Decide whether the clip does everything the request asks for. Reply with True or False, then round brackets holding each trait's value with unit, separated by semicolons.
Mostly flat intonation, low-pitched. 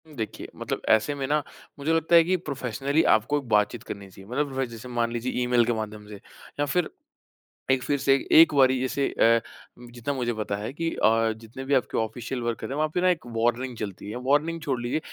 False (4.1 semitones; 125 Hz)